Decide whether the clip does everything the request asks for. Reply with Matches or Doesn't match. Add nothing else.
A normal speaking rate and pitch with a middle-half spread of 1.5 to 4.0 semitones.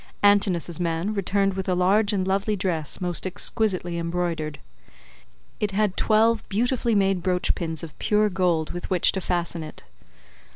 Matches